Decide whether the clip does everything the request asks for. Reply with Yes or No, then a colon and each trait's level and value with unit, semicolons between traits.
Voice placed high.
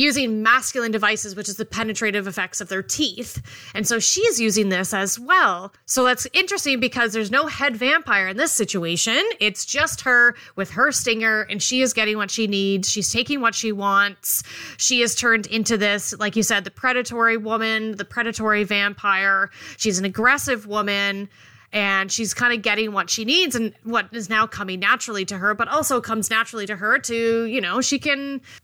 Yes: high, 225 Hz